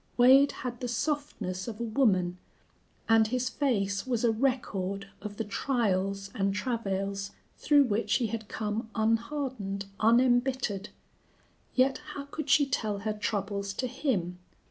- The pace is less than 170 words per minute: Yes, average, 140 wpm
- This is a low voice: No, high, 225 Hz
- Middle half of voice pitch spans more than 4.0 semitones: Yes, average, 4.4 semitones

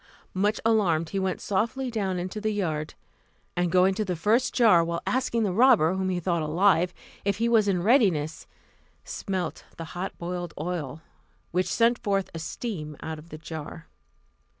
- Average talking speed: Yes, average, 175 wpm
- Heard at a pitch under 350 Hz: Yes, medium, 185 Hz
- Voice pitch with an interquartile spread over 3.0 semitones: Yes, average, 4.3 semitones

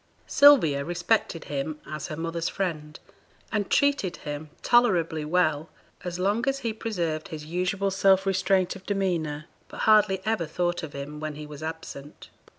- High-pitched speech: No, medium, 175 Hz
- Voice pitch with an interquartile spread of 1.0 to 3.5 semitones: No, average, 4.2 semitones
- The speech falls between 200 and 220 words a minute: No, average, 155 wpm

